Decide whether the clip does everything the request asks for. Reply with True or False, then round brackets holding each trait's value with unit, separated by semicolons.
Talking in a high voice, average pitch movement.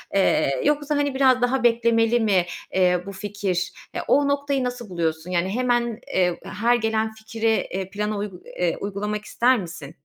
True (215 Hz; 4.5 semitones)